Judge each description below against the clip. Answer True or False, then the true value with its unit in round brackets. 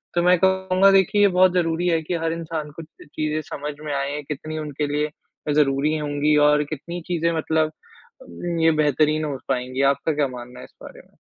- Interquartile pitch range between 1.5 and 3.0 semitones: True (2.4 semitones)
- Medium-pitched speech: True (155 Hz)